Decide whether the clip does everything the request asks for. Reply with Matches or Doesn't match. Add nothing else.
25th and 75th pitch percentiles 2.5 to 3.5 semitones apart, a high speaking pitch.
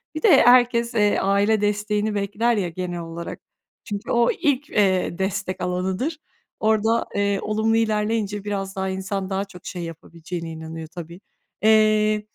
Matches